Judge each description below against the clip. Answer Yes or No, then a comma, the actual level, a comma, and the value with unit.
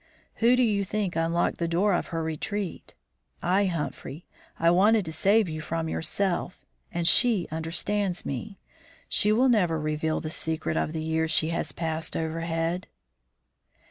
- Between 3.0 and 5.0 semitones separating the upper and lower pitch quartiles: Yes, average, 3.8 semitones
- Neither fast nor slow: Yes, average, 155 wpm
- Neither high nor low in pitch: Yes, medium, 170 Hz